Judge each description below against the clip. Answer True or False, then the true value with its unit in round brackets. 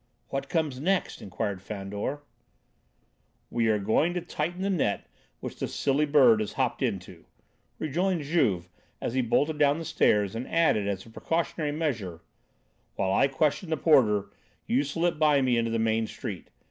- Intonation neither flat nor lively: False (6.7 semitones)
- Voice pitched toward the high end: False (135 Hz)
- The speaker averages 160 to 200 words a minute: True (165 wpm)